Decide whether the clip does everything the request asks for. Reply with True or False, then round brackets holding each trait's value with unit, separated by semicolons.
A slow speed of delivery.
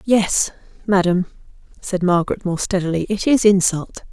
True (130 wpm)